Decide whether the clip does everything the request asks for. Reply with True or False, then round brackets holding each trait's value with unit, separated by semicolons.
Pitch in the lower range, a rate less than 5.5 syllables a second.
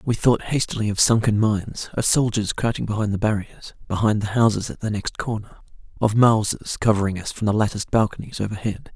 False (110 Hz; 5.8 syllables/s)